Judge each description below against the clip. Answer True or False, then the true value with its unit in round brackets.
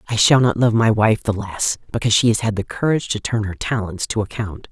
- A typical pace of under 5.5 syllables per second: False (5.9 syllables/s)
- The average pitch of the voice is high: False (110 Hz)